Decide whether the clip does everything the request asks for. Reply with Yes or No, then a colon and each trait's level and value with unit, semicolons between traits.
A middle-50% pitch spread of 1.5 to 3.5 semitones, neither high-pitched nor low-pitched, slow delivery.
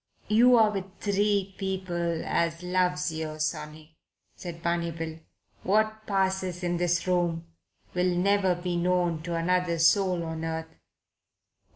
Yes: narrow, 2.4 semitones; medium, 175 Hz; slow, 130 wpm